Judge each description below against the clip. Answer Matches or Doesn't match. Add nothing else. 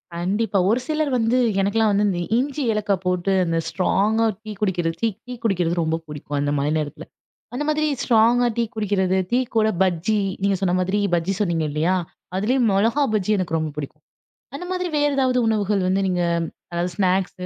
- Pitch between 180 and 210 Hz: Matches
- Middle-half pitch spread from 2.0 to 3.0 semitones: Doesn't match